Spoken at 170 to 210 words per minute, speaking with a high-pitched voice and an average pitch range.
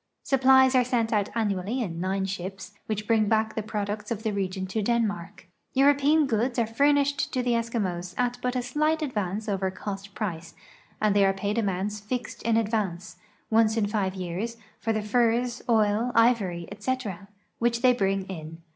Yes: average, 175 wpm; high, 215 Hz; average, 3.6 semitones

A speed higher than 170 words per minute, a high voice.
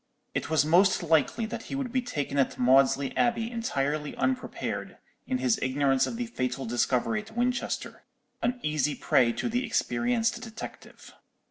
No: average, 155 wpm; high, 215 Hz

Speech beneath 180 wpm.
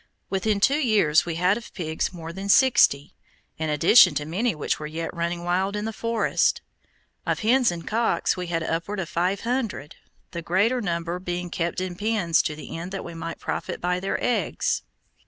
No: average, 190 wpm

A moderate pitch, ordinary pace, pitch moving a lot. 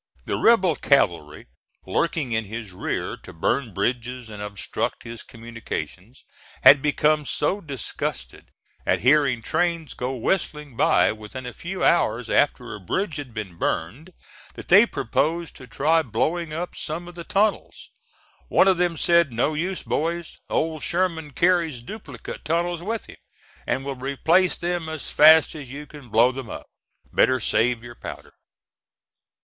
Yes: medium, 145 Hz; average, 155 wpm; wide, 6.2 semitones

